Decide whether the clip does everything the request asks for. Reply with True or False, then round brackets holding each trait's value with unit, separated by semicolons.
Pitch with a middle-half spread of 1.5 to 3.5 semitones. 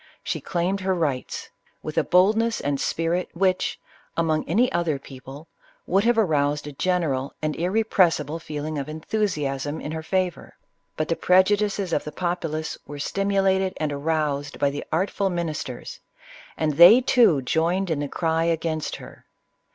False (4.1 semitones)